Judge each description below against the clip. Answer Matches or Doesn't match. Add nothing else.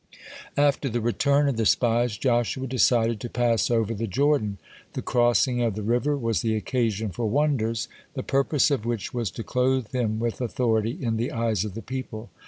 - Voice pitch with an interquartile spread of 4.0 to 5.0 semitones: Doesn't match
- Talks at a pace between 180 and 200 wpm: Matches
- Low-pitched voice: Matches